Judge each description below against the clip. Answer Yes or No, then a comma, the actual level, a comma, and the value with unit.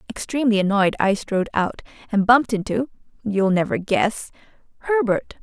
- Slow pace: Yes, slow, 110 wpm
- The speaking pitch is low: No, high, 220 Hz